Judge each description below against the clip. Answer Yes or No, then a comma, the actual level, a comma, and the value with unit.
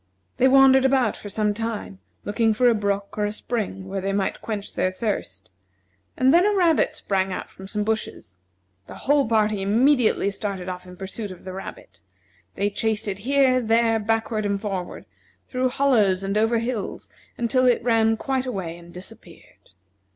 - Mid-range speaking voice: No, high, 215 Hz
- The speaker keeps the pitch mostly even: No, average, 4.0 semitones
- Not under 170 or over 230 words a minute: Yes, average, 175 wpm